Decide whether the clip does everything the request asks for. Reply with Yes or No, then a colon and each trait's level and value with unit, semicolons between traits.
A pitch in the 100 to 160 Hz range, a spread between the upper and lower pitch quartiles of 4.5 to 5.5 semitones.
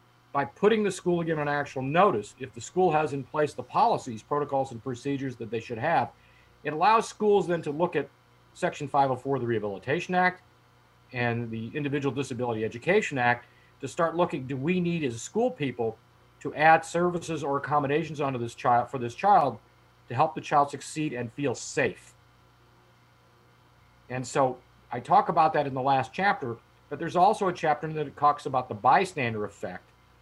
Yes: medium, 140 Hz; average, 4.8 semitones